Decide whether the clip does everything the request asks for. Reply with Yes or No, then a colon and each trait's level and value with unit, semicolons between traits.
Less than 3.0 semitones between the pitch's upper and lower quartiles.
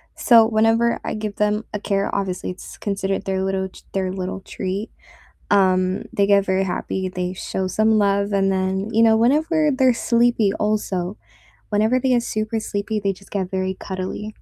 Yes: narrow, 2.6 semitones